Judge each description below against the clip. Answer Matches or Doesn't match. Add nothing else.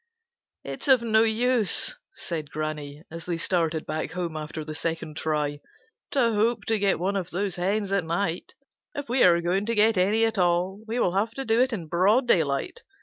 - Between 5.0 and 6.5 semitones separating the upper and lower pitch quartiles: Matches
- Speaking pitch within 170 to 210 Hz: Matches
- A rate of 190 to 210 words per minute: Matches